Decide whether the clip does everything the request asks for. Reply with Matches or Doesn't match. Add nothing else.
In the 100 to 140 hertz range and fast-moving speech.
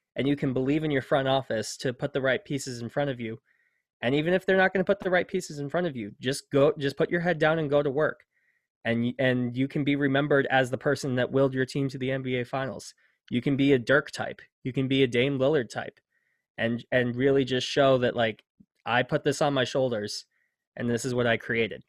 Matches